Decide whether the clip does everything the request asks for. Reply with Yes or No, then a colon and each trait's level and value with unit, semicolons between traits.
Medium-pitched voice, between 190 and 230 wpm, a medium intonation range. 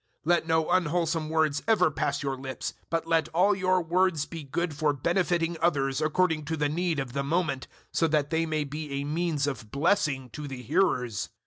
Yes: medium, 155 Hz; average, 200 wpm; average, 3.3 semitones